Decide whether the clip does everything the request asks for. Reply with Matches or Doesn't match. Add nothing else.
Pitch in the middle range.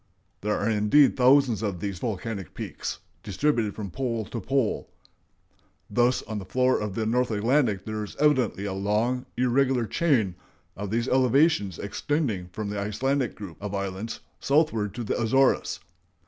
Doesn't match